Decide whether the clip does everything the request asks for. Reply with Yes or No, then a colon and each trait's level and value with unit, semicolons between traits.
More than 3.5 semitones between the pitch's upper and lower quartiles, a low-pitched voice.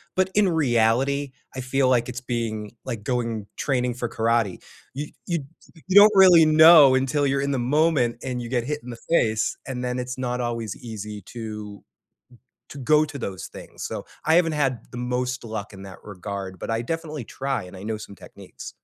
Yes: average, 4.1 semitones; low, 125 Hz